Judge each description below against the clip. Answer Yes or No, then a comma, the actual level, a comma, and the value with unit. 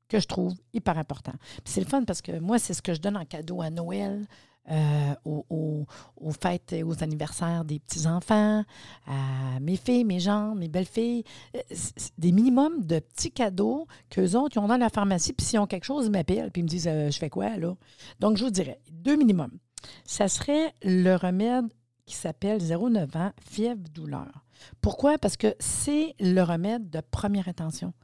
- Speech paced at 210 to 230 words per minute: No, average, 195 wpm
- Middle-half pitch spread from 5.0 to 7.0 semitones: Yes, average, 5.3 semitones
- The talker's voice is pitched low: No, medium, 180 Hz